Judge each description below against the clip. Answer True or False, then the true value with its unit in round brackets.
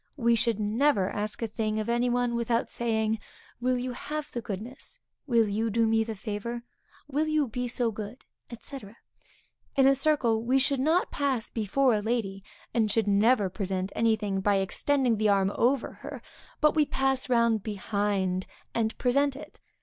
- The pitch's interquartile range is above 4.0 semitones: False (3.5 semitones)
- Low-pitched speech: False (230 Hz)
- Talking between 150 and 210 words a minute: True (175 wpm)